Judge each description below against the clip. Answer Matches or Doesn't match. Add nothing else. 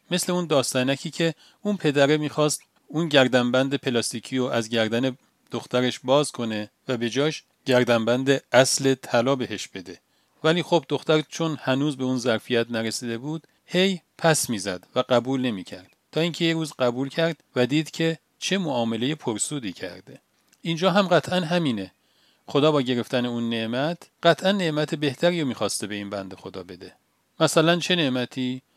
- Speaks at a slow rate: Doesn't match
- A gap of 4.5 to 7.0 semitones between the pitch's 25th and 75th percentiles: Matches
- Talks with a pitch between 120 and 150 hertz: Matches